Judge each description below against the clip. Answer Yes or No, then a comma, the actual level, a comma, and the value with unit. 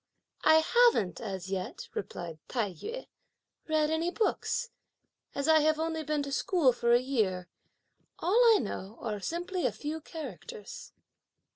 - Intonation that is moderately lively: No, wide, 7.7 semitones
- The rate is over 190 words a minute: No, average, 145 wpm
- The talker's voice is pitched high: Yes, very high, 280 Hz